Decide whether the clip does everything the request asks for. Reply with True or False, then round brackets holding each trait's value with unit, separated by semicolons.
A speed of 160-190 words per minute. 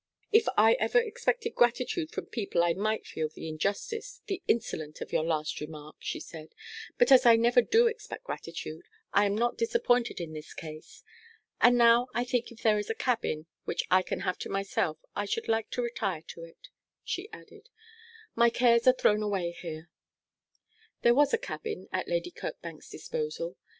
True (180 wpm)